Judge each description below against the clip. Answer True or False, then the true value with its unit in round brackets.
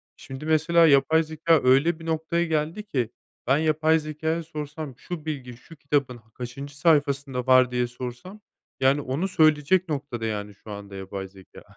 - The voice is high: False (145 Hz)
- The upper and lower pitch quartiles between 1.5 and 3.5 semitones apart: False (4.1 semitones)